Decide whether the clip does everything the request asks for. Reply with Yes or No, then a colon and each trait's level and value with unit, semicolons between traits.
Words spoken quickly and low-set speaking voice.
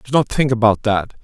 Yes: fast, 240 wpm; low, 115 Hz